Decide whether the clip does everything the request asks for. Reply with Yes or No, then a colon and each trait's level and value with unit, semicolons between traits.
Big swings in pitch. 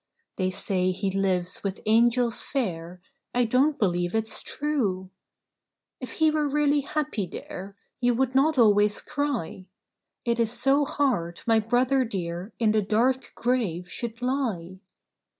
Yes: wide, 5.7 semitones